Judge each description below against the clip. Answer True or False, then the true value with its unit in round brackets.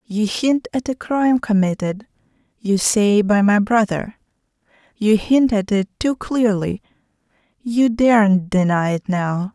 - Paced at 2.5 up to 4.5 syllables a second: True (4.0 syllables/s)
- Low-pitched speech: False (215 Hz)